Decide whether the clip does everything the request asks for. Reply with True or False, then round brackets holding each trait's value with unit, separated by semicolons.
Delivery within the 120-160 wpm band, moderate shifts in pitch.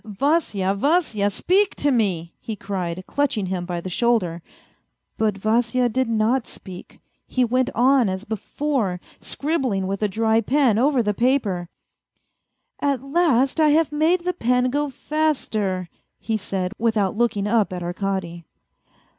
False (150 wpm; 6.0 semitones)